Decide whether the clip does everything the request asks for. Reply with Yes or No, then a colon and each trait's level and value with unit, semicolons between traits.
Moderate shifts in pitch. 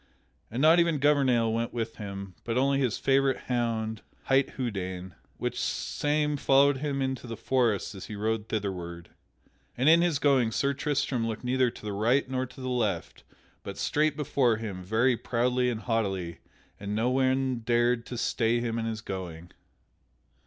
Yes: average, 3.5 semitones